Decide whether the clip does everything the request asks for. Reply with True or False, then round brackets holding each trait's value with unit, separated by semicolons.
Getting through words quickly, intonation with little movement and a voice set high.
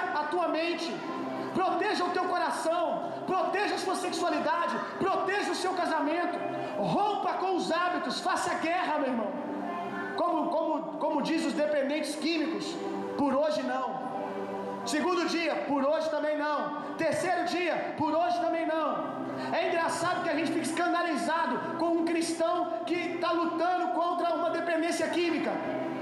True (145 wpm; 1.9 semitones; 335 Hz)